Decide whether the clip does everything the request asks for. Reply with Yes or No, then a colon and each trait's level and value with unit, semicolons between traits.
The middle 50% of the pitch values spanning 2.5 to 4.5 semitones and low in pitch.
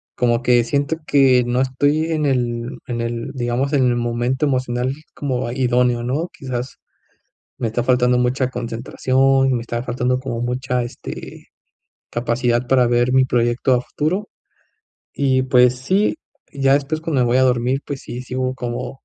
No: narrow, 1.8 semitones; low, 125 Hz